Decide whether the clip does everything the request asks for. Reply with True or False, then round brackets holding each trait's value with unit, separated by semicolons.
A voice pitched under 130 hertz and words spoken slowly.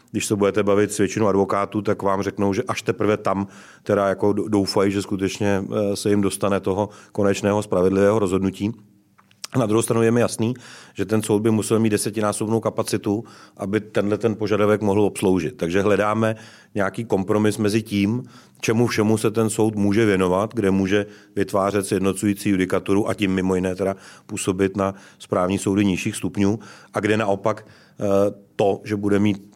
False (105 Hz; 165 wpm)